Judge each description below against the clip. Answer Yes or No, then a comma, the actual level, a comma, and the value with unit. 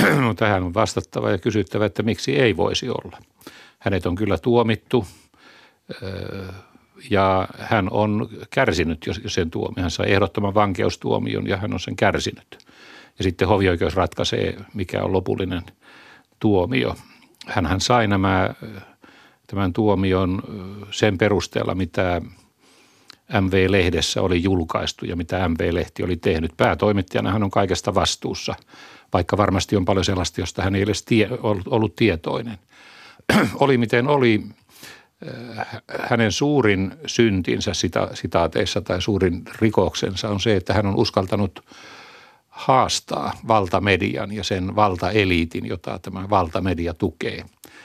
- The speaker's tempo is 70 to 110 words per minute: No, average, 120 wpm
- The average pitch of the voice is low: Yes, low, 100 Hz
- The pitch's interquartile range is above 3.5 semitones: No, narrow, 2.6 semitones